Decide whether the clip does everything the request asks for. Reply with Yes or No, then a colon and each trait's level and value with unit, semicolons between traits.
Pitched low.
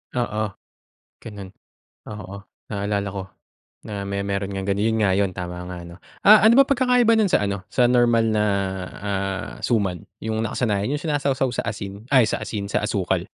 Yes: low, 105 Hz